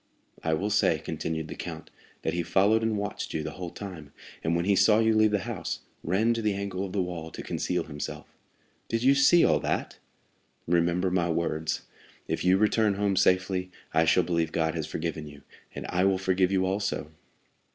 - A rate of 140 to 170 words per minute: No, average, 200 wpm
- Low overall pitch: Yes, very low, 95 Hz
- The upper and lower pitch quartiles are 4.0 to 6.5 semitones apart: No, average, 3.5 semitones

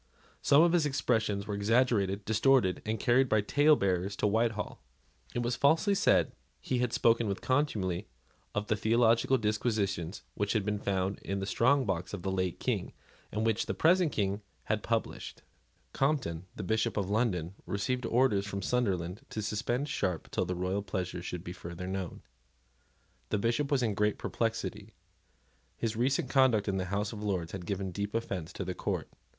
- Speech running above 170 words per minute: Yes, average, 180 wpm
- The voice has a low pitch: Yes, low, 105 Hz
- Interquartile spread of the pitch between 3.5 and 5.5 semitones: Yes, average, 3.9 semitones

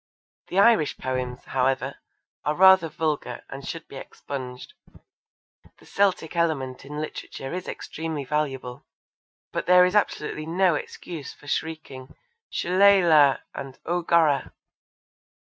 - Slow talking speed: Yes, slow, 120 wpm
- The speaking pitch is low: No, medium, 155 Hz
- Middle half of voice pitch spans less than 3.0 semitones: No, average, 4.4 semitones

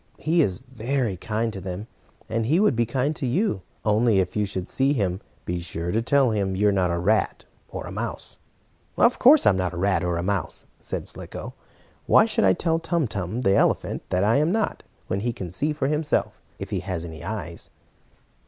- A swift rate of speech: Yes, fast, 210 wpm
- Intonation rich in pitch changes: Yes, wide, 6.4 semitones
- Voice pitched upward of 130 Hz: No, low, 105 Hz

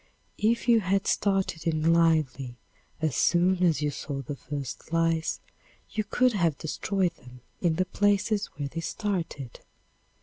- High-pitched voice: No, medium, 165 Hz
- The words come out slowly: No, average, 145 wpm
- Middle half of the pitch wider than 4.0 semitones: Yes, average, 4.8 semitones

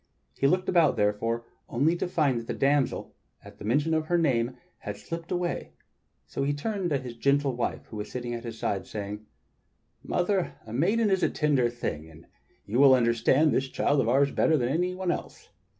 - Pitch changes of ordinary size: No, wide, 5.9 semitones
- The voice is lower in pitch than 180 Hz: Yes, medium, 140 Hz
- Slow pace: No, average, 200 wpm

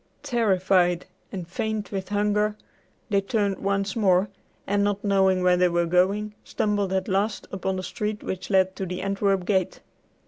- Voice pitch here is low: No, high, 195 Hz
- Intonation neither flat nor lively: No, narrow, 1.8 semitones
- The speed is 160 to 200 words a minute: Yes, average, 165 wpm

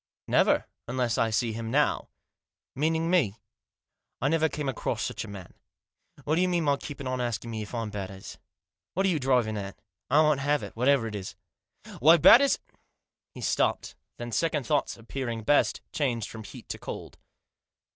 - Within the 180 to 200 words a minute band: Yes, average, 185 wpm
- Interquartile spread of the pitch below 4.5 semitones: No, average, 4.9 semitones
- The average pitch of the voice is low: Yes, low, 130 Hz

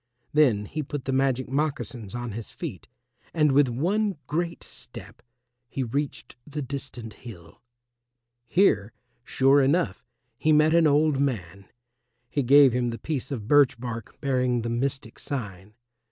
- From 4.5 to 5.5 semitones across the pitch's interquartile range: No, average, 3.8 semitones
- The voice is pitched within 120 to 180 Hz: Yes, low, 135 Hz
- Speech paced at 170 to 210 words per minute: No, average, 145 wpm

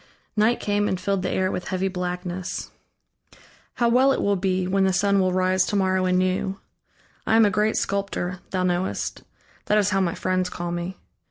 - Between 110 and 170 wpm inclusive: No, average, 190 wpm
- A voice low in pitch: No, medium, 185 Hz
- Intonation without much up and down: Yes, narrow, 1.5 semitones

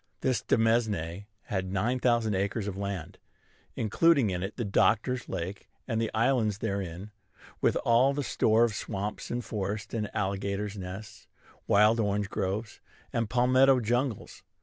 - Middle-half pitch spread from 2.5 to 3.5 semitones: Yes, average, 3.0 semitones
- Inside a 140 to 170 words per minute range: Yes, average, 145 wpm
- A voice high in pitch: No, low, 110 Hz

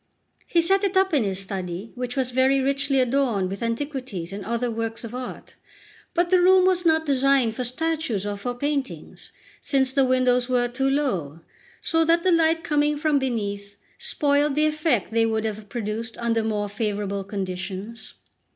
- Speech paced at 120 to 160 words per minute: No, average, 175 wpm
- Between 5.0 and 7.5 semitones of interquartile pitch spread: Yes, wide, 5.5 semitones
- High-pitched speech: Yes, very high, 250 Hz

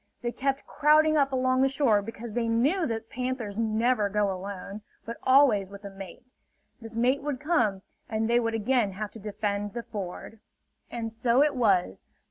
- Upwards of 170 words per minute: Yes, average, 180 wpm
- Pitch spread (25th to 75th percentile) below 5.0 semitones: Yes, average, 3.9 semitones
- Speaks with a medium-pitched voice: No, high, 230 Hz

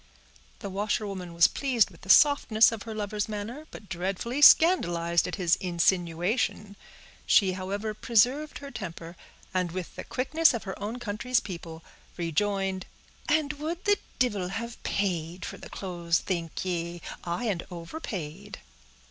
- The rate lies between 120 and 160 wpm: Yes, average, 140 wpm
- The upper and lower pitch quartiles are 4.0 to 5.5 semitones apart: Yes, average, 5.1 semitones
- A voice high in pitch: Yes, high, 200 Hz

